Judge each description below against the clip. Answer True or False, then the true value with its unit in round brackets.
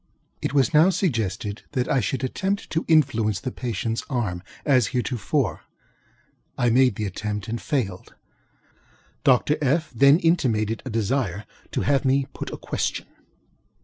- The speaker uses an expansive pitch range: False (4.4 semitones)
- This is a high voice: False (125 Hz)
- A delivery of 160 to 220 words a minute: False (145 wpm)